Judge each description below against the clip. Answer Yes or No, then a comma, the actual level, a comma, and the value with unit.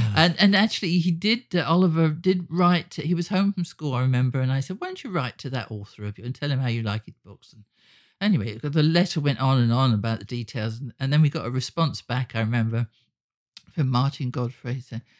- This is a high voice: No, low, 135 Hz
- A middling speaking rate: No, fast, 240 wpm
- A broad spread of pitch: Yes, wide, 6.4 semitones